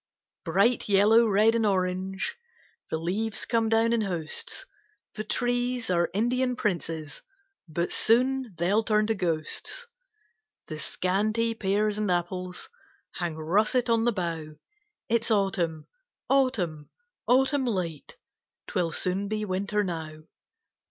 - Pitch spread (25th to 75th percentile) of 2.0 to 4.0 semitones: No, average, 4.6 semitones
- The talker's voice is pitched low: No, high, 205 Hz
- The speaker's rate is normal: No, slow, 120 wpm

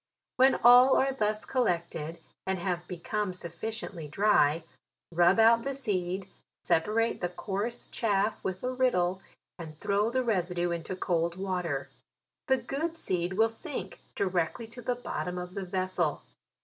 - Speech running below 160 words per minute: Yes, average, 150 wpm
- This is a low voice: No, high, 190 Hz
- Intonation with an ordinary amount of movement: Yes, average, 4.6 semitones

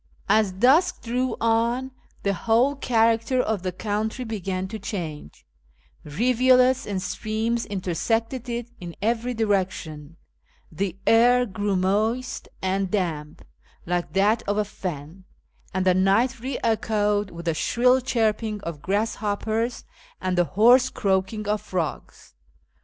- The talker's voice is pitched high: Yes, high, 210 Hz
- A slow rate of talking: Yes, slow, 130 wpm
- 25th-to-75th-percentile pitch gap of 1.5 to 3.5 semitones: No, average, 3.9 semitones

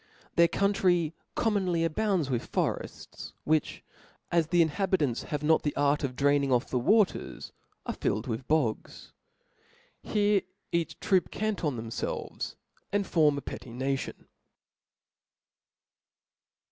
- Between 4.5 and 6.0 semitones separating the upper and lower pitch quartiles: Yes, wide, 5.4 semitones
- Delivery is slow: Yes, slow, 120 wpm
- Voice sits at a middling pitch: Yes, medium, 155 Hz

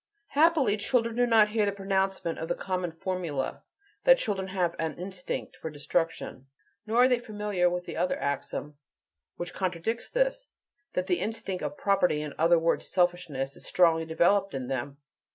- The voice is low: No, medium, 185 Hz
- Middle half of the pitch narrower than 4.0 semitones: No, average, 4.3 semitones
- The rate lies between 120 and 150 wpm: No, average, 170 wpm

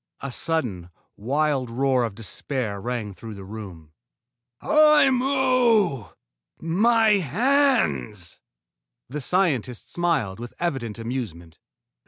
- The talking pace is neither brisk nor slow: No, slow, 95 wpm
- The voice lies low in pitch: Yes, low, 130 Hz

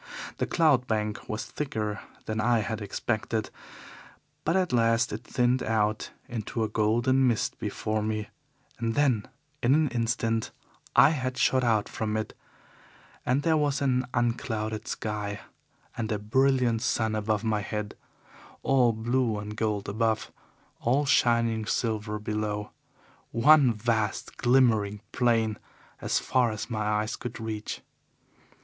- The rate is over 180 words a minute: No, slow, 135 wpm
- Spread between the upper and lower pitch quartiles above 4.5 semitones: No, average, 2.7 semitones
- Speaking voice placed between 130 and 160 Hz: No, low, 115 Hz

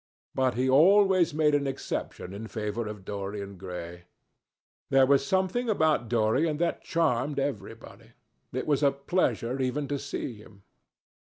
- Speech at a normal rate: Yes, average, 145 wpm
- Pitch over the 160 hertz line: No, low, 130 Hz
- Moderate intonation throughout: No, wide, 5.8 semitones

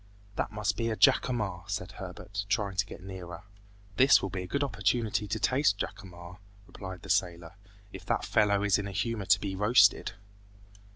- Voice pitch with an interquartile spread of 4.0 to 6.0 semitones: No, narrow, 2.5 semitones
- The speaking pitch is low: Yes, low, 100 Hz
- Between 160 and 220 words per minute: Yes, average, 180 wpm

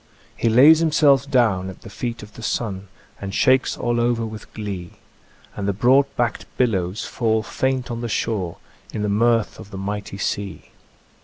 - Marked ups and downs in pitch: No, average, 3.3 semitones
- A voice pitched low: Yes, low, 110 Hz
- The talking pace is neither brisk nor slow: Yes, average, 175 wpm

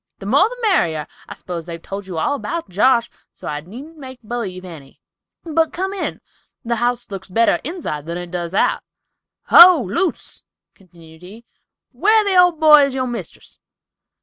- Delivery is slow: No, average, 165 wpm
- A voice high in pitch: Yes, high, 235 Hz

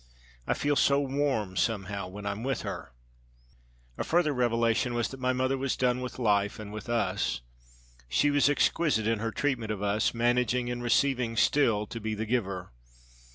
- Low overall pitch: Yes, low, 120 Hz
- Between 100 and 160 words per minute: No, average, 175 wpm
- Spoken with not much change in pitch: No, average, 3.5 semitones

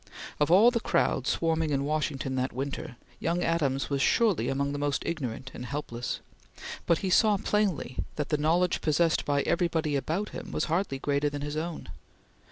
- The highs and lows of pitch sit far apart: No, average, 3.4 semitones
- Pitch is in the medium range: Yes, medium, 150 Hz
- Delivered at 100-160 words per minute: No, average, 175 wpm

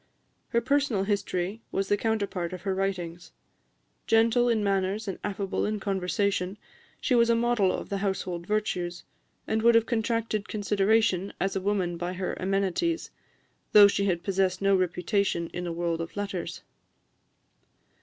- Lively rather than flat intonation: No, average, 3.0 semitones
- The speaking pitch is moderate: No, high, 195 Hz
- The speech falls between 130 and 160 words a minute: Yes, average, 155 wpm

